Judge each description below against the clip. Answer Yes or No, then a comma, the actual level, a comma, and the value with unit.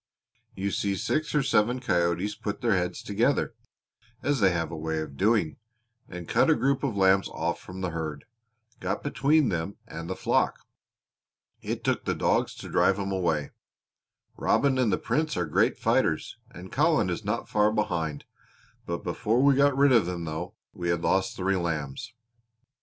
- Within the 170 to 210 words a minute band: Yes, average, 175 wpm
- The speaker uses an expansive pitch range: Yes, wide, 6.0 semitones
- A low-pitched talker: Yes, very low, 95 Hz